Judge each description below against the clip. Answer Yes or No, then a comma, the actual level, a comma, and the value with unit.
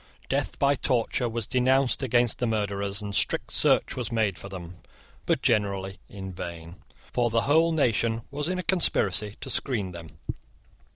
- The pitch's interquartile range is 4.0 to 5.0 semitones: Yes, average, 4.6 semitones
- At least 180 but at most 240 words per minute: No, average, 165 wpm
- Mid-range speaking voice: No, low, 110 Hz